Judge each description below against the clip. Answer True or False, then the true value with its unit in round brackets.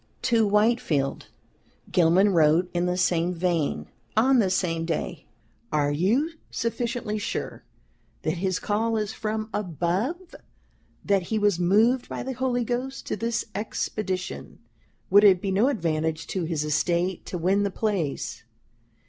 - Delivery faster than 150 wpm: False (140 wpm)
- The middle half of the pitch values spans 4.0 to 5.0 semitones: True (4.5 semitones)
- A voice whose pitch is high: True (195 Hz)